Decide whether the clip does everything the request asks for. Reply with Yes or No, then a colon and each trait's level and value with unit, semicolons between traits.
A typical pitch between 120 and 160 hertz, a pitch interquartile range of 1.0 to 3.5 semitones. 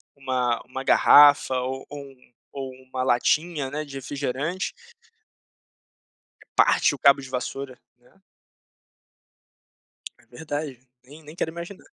Yes: low, 135 Hz; narrow, 2.5 semitones